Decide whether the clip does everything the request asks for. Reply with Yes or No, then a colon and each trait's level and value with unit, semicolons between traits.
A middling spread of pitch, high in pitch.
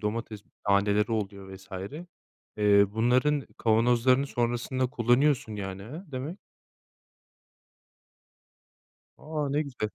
No: average, 4.0 semitones; low, 120 Hz